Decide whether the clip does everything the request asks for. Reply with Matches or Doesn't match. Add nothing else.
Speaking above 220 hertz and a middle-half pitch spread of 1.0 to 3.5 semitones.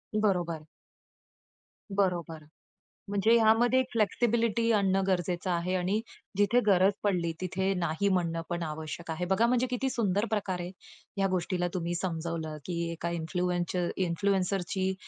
Doesn't match